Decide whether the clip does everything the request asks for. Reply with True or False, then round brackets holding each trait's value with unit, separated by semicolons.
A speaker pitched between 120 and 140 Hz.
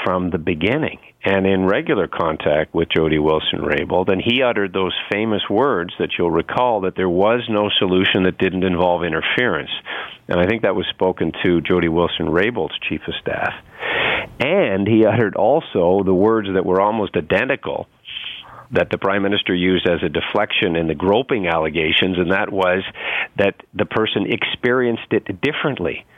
False (95 Hz)